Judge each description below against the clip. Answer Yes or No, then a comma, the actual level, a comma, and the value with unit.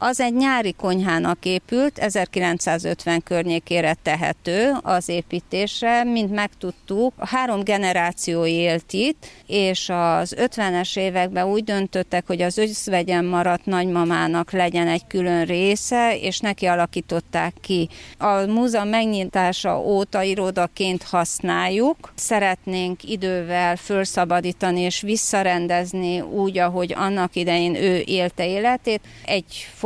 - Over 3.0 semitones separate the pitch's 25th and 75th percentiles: No, narrow, 2.6 semitones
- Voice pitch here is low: No, medium, 185 Hz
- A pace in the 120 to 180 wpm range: No, average, 110 wpm